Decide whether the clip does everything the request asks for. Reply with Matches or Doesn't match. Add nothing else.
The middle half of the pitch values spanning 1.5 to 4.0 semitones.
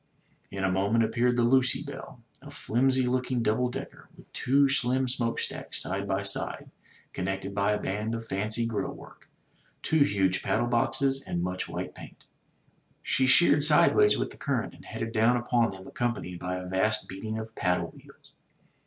Doesn't match